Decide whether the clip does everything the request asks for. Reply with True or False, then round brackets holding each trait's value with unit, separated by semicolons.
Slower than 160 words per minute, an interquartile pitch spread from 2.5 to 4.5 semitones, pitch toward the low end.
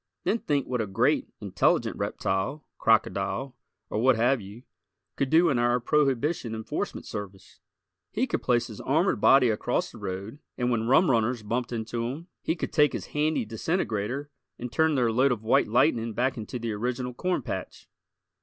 False (175 wpm; 3.8 semitones; 125 Hz)